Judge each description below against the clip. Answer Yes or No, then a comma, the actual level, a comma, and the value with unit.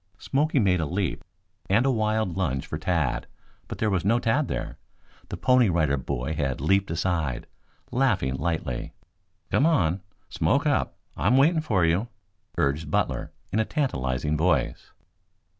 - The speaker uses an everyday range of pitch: No, wide, 6.8 semitones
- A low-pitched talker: Yes, very low, 90 Hz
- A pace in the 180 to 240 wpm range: No, average, 150 wpm